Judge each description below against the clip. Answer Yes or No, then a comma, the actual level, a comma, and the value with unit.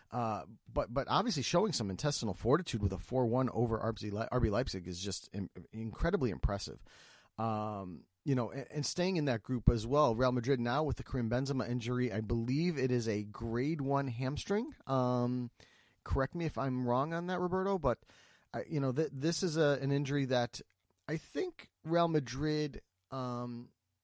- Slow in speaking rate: No, average, 180 wpm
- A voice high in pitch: No, low, 125 Hz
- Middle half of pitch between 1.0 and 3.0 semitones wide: No, average, 4.2 semitones